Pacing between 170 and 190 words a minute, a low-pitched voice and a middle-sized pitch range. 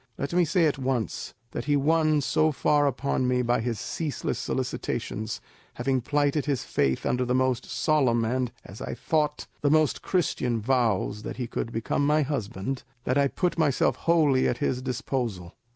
Yes: average, 175 wpm; low, 130 Hz; average, 3.7 semitones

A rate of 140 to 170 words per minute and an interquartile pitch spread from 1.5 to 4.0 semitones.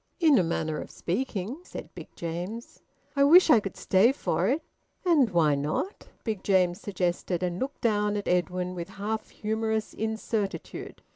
No: average, 160 wpm; average, 4.5 semitones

